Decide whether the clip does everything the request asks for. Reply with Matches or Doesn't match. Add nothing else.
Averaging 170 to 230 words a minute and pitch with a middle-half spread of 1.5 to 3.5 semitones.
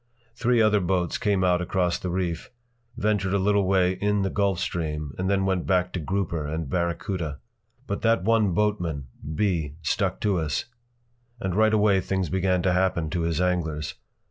Matches